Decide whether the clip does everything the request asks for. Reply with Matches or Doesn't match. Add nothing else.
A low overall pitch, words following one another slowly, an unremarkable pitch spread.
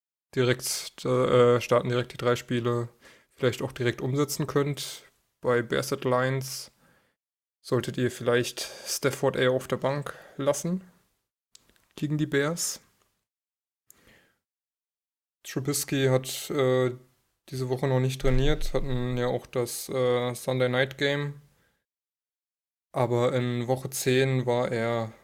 Doesn't match